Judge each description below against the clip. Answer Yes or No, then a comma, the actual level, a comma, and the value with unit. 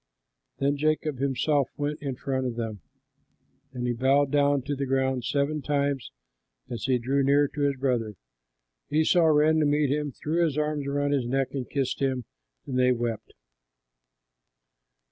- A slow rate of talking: No, average, 165 wpm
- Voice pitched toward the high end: No, medium, 140 Hz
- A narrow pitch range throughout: Yes, narrow, 2.2 semitones